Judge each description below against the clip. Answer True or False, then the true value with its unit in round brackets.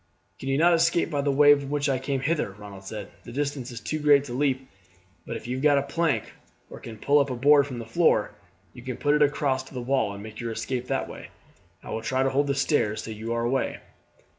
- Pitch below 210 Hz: True (135 Hz)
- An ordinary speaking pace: False (260 wpm)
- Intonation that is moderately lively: True (3.5 semitones)